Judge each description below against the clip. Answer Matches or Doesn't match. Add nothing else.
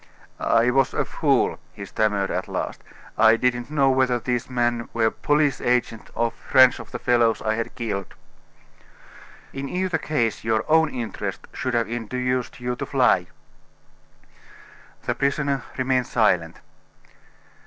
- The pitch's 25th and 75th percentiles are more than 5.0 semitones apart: Doesn't match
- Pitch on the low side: Matches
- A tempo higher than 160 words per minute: Doesn't match